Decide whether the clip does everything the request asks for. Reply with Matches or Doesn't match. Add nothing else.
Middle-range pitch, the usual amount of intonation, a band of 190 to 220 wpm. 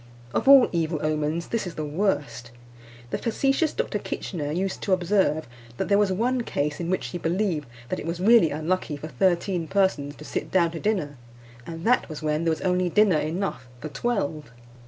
Matches